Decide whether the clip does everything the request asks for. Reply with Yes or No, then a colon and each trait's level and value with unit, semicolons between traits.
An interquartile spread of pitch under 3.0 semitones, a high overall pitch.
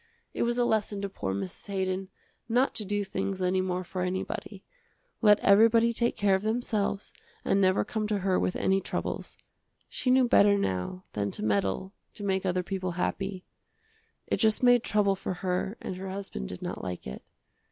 Yes: narrow, 2.5 semitones; high, 195 Hz